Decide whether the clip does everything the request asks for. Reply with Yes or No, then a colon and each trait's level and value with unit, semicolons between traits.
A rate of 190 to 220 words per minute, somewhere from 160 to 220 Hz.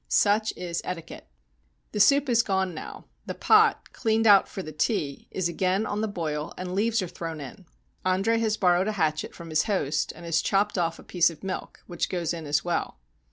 Yes: fast, 205 wpm; medium, 185 Hz